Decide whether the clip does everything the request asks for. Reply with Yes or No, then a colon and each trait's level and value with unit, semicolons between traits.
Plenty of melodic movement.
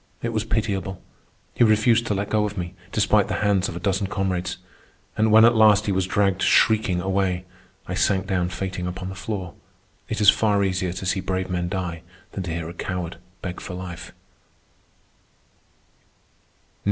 No: narrow, 2.5 semitones